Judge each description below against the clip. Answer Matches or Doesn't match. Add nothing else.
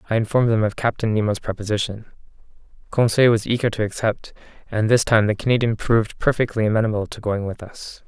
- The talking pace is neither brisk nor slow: Matches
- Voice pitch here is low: Matches